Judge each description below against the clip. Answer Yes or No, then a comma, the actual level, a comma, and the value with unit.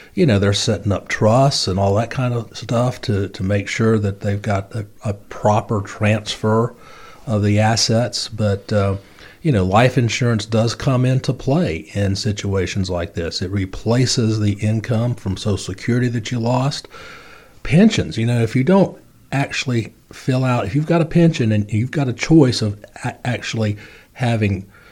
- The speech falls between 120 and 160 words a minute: No, average, 175 wpm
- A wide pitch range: No, average, 3.4 semitones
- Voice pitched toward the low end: Yes, low, 110 Hz